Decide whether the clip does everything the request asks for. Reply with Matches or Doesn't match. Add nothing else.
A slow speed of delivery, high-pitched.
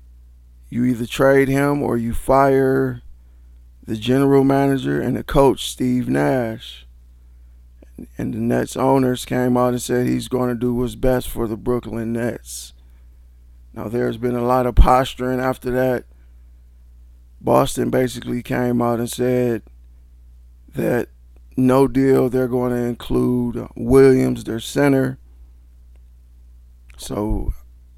Doesn't match